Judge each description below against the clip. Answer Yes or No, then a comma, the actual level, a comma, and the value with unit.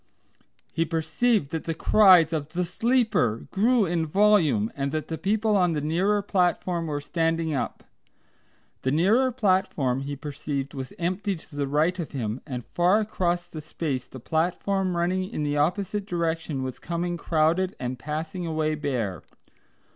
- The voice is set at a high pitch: No, medium, 165 Hz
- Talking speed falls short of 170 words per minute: Yes, average, 160 wpm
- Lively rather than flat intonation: No, average, 4.4 semitones